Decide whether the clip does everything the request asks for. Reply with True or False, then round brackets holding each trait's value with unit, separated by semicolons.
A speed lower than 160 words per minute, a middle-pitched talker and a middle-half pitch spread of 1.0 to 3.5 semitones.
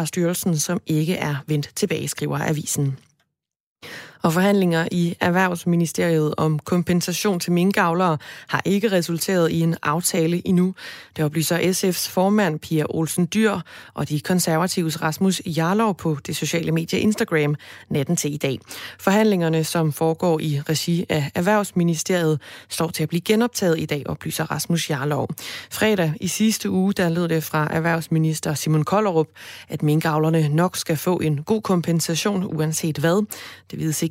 True (150 wpm; 165 Hz; 2.8 semitones)